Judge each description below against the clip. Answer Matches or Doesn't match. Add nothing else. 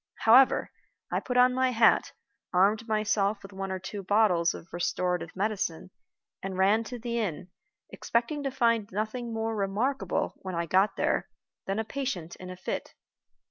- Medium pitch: Doesn't match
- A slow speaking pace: Doesn't match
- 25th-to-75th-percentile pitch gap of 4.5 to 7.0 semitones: Doesn't match